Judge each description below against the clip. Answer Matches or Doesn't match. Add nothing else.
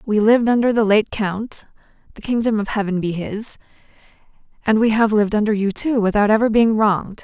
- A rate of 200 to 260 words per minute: Doesn't match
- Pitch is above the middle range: Matches